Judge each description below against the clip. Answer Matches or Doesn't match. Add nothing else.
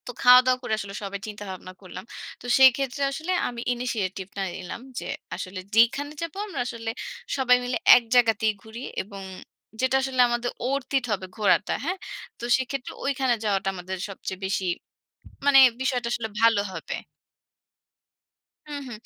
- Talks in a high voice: Matches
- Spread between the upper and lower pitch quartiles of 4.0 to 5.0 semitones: Matches